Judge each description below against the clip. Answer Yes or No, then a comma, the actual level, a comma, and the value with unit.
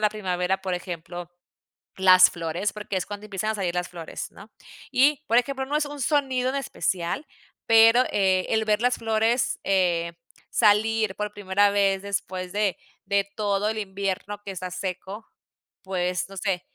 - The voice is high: Yes, high, 200 Hz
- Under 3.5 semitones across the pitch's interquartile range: Yes, average, 3.1 semitones